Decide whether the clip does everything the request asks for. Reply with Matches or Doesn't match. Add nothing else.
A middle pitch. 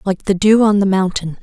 Doesn't match